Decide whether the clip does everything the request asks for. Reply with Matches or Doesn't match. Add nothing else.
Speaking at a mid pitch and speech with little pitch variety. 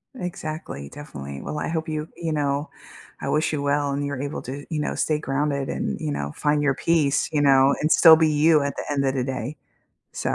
Matches